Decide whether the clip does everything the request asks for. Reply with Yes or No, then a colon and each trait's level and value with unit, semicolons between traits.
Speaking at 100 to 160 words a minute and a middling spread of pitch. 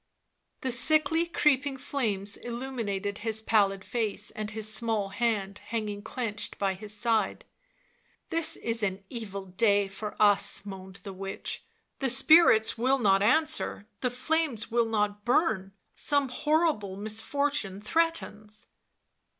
Yes: slow, 135 wpm; average, 4.4 semitones